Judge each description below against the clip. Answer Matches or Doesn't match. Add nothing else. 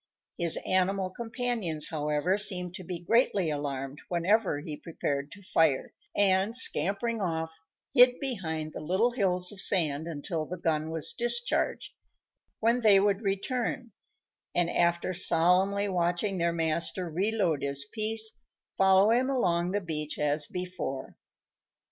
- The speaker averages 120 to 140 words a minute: Matches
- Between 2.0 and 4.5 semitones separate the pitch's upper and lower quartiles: Matches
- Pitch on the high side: Doesn't match